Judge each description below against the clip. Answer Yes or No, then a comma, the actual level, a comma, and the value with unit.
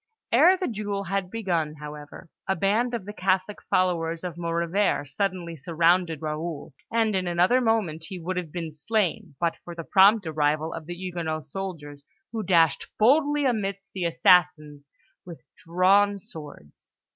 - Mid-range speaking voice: Yes, medium, 175 Hz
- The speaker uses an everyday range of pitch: Yes, average, 3.6 semitones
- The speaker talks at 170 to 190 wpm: No, average, 155 wpm